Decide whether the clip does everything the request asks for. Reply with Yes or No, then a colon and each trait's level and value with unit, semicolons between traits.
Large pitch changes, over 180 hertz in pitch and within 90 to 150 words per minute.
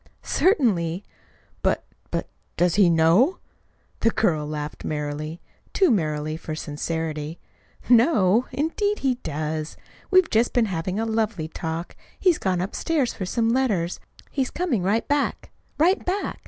Yes: wide, 8.0 semitones; high, 190 Hz; slow, 135 wpm